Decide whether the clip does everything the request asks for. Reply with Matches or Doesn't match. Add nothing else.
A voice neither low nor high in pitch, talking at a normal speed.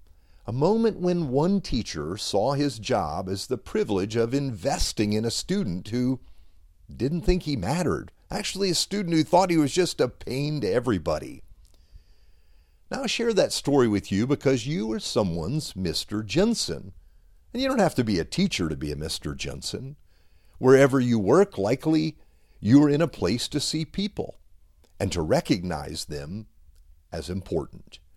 Doesn't match